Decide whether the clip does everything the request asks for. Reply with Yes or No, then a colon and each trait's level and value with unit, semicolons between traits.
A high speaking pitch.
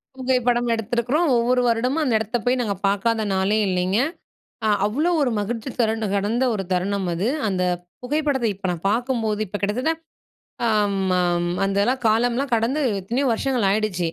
Yes: high, 225 Hz